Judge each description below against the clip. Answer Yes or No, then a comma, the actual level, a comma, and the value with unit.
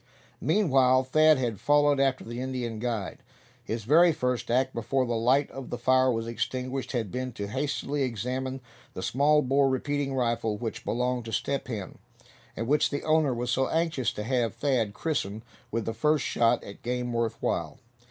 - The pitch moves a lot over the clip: No, average, 2.8 semitones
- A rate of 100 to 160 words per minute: No, average, 180 wpm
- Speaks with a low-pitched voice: Yes, low, 125 Hz